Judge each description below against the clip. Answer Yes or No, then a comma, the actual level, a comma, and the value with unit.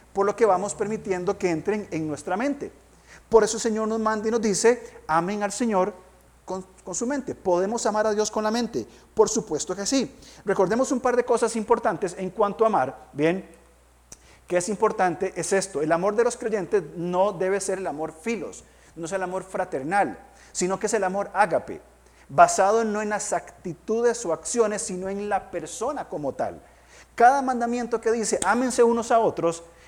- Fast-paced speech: Yes, fast, 195 wpm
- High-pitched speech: Yes, high, 205 Hz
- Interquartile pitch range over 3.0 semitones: Yes, average, 3.7 semitones